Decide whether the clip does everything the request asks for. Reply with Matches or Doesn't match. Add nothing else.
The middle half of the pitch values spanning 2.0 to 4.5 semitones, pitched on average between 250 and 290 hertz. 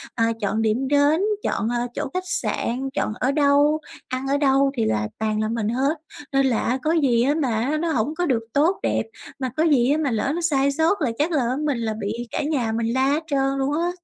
Matches